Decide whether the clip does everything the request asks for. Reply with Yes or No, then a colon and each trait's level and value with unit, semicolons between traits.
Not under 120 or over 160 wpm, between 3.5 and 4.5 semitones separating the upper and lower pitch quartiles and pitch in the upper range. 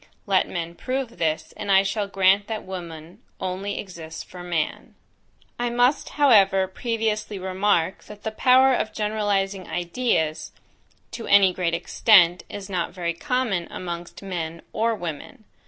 Yes: average, 140 wpm; average, 3.8 semitones; high, 195 Hz